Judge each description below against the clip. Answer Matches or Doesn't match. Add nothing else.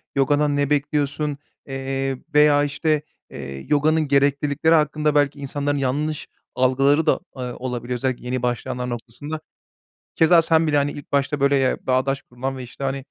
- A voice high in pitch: Doesn't match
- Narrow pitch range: Matches